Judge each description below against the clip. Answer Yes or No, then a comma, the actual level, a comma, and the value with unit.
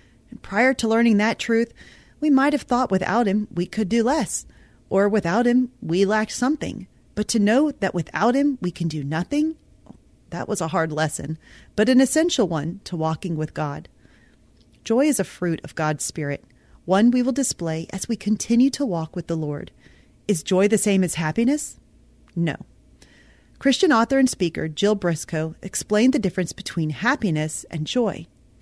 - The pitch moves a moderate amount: No, wide, 6.6 semitones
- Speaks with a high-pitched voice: Yes, high, 195 Hz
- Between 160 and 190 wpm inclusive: Yes, average, 175 wpm